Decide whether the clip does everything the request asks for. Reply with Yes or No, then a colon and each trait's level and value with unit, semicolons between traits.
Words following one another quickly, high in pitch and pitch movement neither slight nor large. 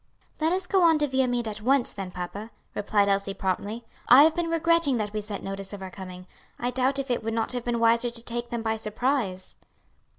Yes: fast, 225 wpm; high, 230 Hz; average, 4.6 semitones